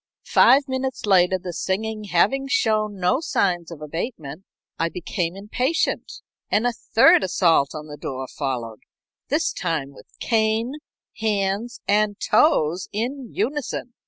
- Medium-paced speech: No, slow, 130 wpm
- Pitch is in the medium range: No, high, 200 Hz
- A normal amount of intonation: No, wide, 5.8 semitones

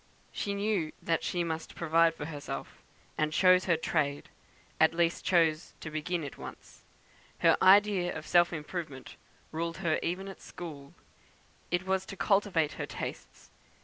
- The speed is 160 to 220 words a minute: No, average, 150 wpm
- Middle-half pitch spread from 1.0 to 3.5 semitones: Yes, average, 2.8 semitones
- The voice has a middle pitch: Yes, medium, 170 Hz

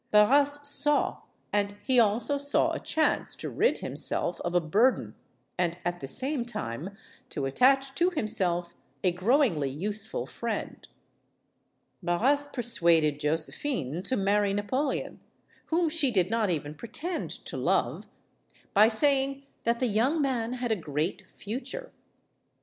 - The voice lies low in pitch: No, high, 220 Hz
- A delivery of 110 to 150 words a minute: Yes, slow, 135 wpm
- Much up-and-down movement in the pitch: Yes, wide, 7.7 semitones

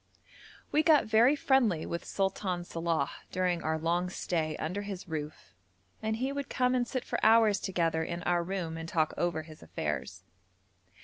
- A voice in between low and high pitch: Yes, medium, 180 Hz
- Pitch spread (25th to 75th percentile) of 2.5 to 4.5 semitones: No, average, 5.1 semitones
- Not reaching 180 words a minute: Yes, average, 170 wpm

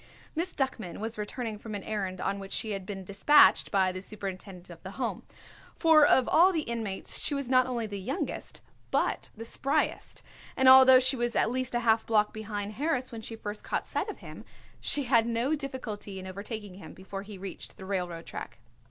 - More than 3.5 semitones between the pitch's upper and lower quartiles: Yes, average, 4.6 semitones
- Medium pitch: No, high, 220 Hz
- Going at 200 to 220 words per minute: Yes, fast, 205 wpm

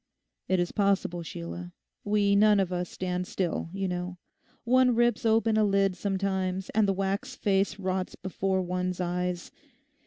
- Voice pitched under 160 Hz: No, high, 190 Hz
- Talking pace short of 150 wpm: No, average, 155 wpm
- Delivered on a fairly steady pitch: Yes, narrow, 2.1 semitones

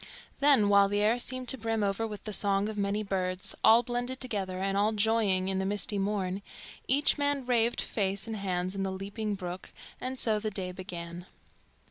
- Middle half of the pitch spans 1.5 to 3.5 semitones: Yes, average, 2.8 semitones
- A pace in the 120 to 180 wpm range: No, average, 195 wpm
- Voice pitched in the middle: No, high, 205 Hz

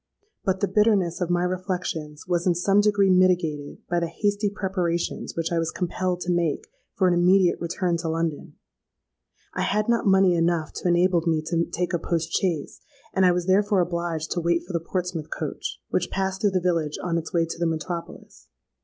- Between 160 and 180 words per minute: No, average, 195 wpm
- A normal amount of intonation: No, narrow, 2.1 semitones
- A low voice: No, medium, 175 Hz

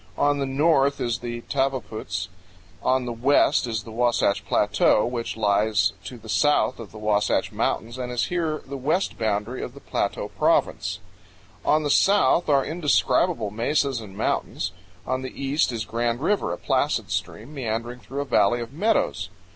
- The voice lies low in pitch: Yes, low, 125 Hz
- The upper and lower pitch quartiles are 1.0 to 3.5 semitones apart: No, average, 4.1 semitones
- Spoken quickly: No, average, 170 wpm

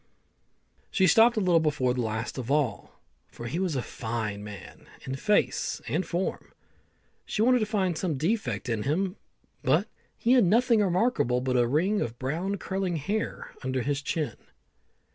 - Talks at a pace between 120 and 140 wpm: No, average, 165 wpm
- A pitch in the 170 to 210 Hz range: No, medium, 160 Hz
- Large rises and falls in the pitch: Yes, wide, 7.9 semitones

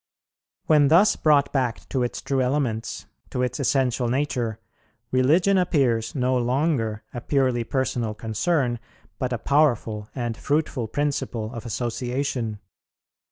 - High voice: No, low, 125 Hz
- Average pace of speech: No, slow, 125 wpm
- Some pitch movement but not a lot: Yes, average, 3.4 semitones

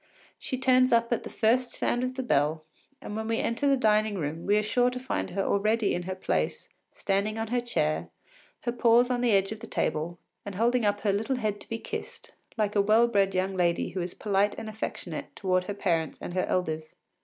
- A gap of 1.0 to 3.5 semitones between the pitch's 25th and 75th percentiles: No, average, 4.0 semitones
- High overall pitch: Yes, high, 210 Hz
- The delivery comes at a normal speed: No, fast, 225 wpm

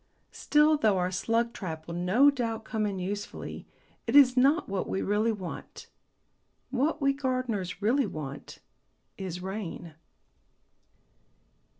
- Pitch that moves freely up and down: Yes, wide, 5.7 semitones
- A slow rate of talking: Yes, slow, 125 wpm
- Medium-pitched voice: No, high, 215 Hz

